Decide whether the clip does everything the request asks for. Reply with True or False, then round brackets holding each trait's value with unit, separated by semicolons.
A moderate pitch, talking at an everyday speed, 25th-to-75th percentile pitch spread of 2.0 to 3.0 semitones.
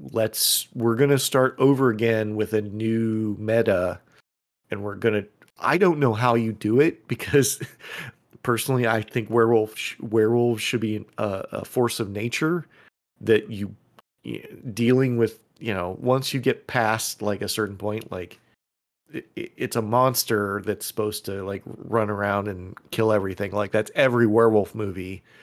False (110 Hz; 155 wpm; 2.5 semitones)